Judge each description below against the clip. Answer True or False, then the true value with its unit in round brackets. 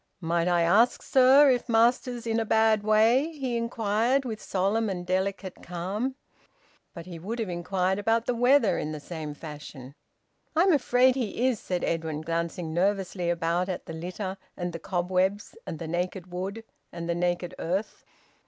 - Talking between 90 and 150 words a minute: False (170 wpm)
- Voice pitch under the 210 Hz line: True (190 Hz)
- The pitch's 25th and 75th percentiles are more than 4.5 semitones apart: True (4.9 semitones)